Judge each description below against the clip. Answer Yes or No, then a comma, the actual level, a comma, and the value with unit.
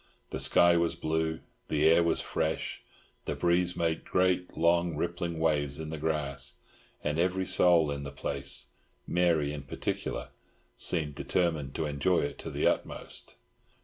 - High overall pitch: No, very low, 80 Hz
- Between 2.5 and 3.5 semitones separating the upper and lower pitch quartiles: Yes, average, 2.9 semitones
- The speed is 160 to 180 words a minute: No, average, 145 wpm